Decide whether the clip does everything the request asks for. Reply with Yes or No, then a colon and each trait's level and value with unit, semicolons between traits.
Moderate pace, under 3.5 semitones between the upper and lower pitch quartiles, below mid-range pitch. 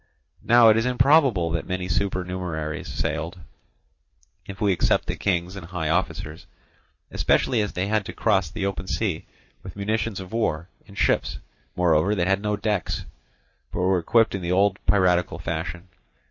Yes: average, 160 wpm; average, 2.9 semitones; very low, 95 Hz